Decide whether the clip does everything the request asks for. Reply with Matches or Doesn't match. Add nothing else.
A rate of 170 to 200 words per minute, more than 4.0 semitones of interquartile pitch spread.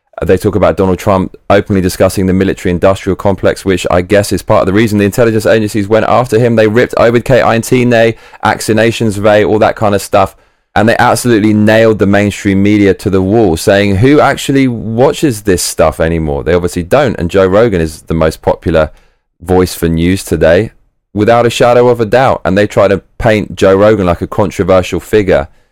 Doesn't match